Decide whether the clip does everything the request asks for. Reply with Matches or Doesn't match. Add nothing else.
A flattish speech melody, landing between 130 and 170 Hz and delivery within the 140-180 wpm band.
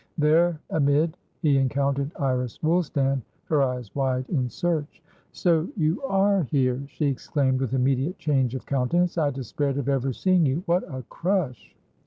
Doesn't match